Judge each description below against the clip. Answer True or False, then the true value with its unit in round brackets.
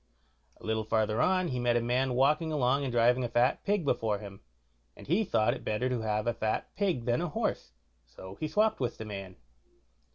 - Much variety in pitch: False (4.6 semitones)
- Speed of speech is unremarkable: False (215 wpm)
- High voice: False (120 Hz)